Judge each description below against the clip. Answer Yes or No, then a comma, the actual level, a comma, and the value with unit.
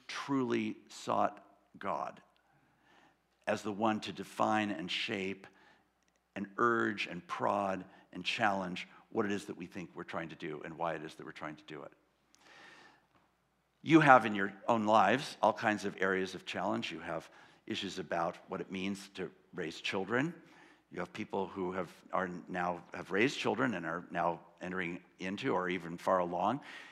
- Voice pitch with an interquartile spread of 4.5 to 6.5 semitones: No, average, 3.2 semitones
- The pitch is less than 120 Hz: Yes, low, 100 Hz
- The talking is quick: No, average, 170 wpm